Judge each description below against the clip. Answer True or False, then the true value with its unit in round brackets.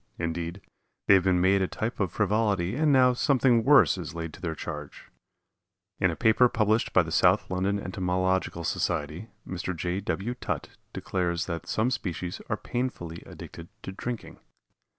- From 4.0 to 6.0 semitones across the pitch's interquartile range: True (4.3 semitones)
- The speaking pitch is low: True (95 Hz)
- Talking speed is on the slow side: False (165 wpm)